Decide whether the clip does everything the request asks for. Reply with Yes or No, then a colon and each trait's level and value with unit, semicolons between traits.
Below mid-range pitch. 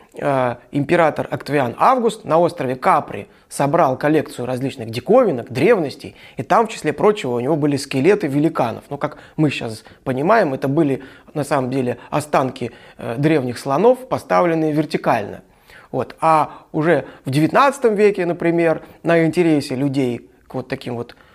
No: medium, 150 Hz